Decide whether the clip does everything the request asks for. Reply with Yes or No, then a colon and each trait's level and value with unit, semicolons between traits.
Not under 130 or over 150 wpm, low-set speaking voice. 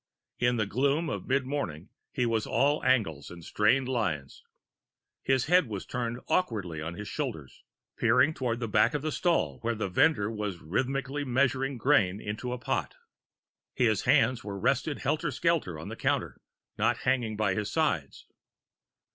No: average, 165 wpm; low, 120 Hz